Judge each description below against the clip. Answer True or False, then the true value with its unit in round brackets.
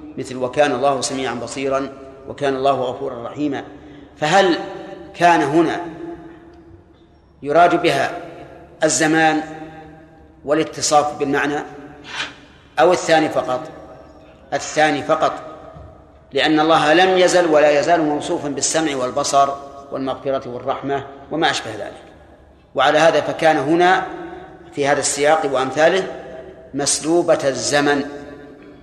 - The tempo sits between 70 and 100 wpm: True (95 wpm)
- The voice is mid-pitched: True (150 Hz)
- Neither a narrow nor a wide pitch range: True (3.2 semitones)